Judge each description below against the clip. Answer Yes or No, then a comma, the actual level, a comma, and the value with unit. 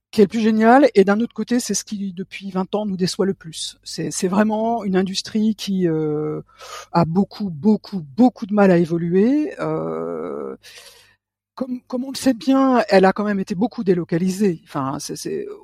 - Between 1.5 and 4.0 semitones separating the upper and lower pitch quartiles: No, average, 4.5 semitones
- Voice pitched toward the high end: Yes, high, 200 Hz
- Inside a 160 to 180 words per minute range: No, average, 195 wpm